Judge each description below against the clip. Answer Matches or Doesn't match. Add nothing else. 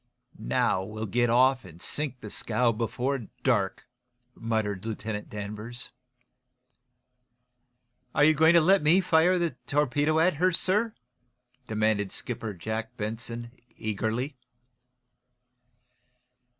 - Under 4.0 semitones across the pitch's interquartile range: Doesn't match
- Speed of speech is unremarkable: Doesn't match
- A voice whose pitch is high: Doesn't match